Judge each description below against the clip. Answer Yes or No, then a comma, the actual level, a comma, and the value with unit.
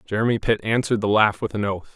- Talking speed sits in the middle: No, fast, 245 wpm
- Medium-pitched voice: No, low, 105 Hz